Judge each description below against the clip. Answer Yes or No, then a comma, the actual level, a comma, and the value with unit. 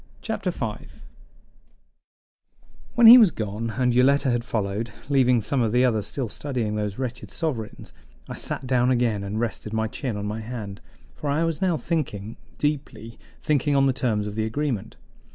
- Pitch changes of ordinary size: Yes, average, 4.4 semitones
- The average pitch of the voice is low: Yes, low, 120 Hz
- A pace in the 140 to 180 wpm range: Yes, average, 170 wpm